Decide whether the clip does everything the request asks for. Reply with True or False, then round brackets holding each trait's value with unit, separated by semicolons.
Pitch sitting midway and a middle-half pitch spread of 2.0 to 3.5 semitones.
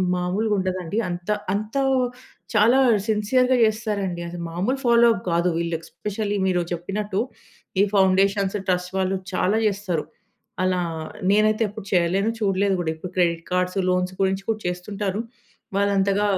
False (195 Hz; 2.7 semitones)